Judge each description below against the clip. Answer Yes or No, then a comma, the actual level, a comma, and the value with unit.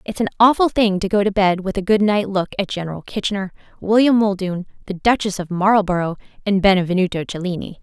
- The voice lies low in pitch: No, high, 195 Hz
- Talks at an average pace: Yes, average, 190 wpm